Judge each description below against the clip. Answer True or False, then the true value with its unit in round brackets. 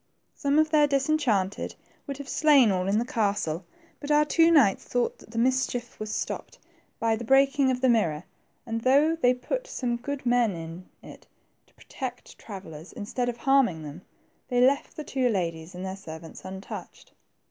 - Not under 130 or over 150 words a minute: False (195 wpm)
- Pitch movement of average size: False (6.2 semitones)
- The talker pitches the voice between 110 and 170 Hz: False (240 Hz)